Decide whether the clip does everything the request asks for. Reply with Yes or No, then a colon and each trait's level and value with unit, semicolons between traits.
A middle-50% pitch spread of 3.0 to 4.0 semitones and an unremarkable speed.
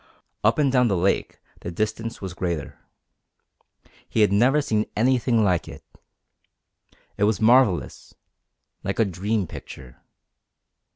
No: average, 3.7 semitones; slow, 125 wpm